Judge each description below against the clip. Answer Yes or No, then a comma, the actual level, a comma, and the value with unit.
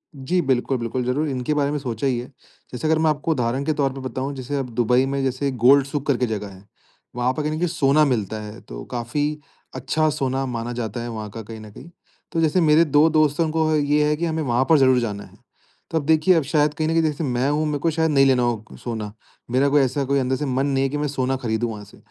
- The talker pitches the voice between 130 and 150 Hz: Yes, low, 135 Hz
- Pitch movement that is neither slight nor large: Yes, average, 3.6 semitones